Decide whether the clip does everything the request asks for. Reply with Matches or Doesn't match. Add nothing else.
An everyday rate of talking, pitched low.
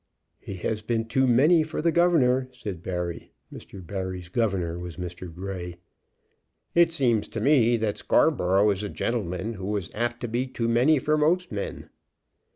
Matches